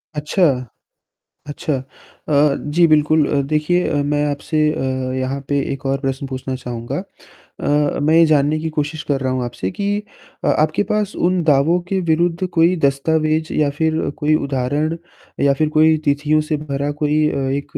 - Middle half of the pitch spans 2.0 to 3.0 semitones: Yes, narrow, 2.4 semitones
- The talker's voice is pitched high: No, medium, 150 Hz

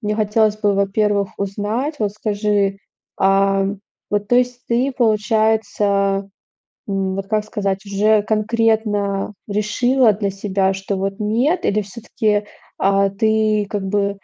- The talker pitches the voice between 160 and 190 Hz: No, high, 205 Hz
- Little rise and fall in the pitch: Yes, narrow, 1.7 semitones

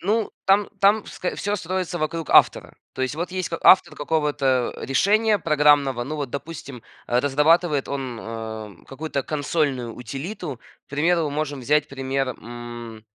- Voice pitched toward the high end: No, medium, 145 Hz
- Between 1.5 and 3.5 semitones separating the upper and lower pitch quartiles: No, average, 4.4 semitones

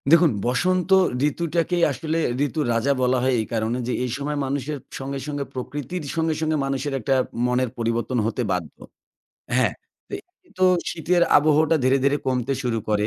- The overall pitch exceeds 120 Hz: Yes, medium, 140 Hz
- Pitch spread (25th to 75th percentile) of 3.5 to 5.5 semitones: Yes, average, 4.1 semitones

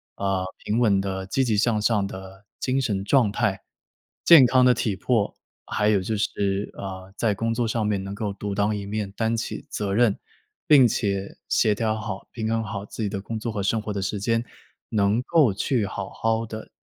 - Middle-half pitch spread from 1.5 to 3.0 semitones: Yes, narrow, 2.6 semitones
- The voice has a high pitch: No, low, 105 Hz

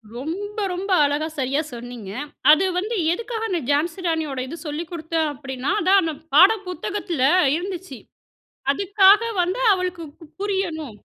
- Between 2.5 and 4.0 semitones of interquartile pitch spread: No, average, 4.8 semitones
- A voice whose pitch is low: No, very high, 335 Hz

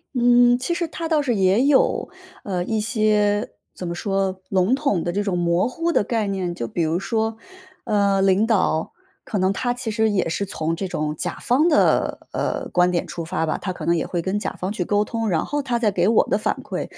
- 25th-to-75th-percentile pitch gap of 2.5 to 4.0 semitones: No, average, 4.6 semitones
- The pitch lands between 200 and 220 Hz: Yes, high, 205 Hz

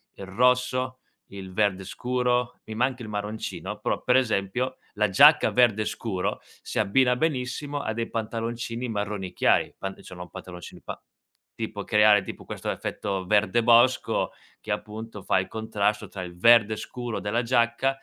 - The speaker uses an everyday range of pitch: Yes, average, 3.3 semitones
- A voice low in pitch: Yes, low, 110 Hz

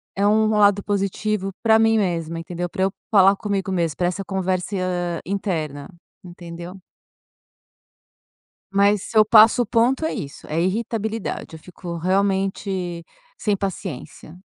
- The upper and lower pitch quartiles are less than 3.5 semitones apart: Yes, average, 3.0 semitones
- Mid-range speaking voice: No, high, 195 Hz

